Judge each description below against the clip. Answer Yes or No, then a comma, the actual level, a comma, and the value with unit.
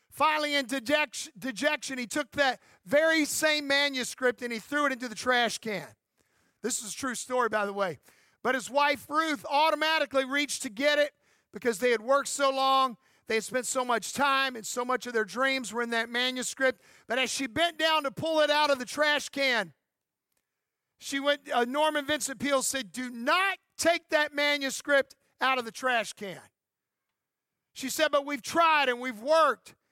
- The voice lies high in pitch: Yes, very high, 270 Hz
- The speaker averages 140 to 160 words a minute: No, average, 190 wpm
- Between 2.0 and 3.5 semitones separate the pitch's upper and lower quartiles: Yes, average, 3.0 semitones